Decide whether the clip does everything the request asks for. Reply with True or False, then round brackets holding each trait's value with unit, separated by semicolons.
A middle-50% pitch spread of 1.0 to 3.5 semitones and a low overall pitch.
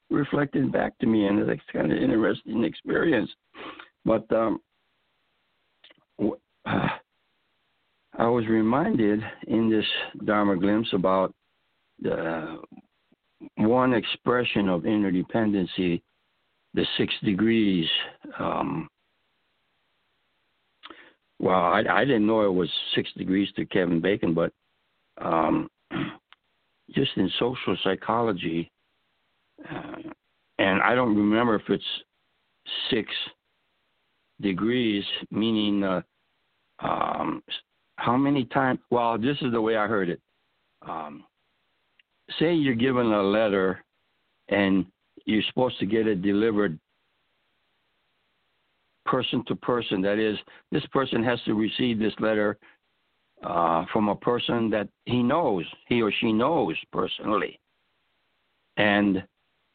True (2.5 semitones; 105 Hz)